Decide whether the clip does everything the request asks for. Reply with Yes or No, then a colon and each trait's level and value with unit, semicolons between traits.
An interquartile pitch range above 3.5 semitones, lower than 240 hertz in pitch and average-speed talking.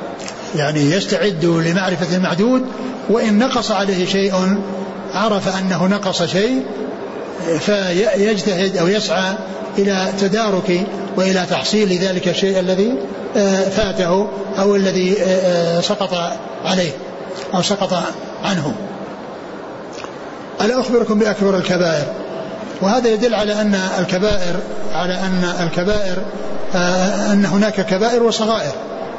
No: narrow, 2.4 semitones; high, 190 Hz; average, 95 wpm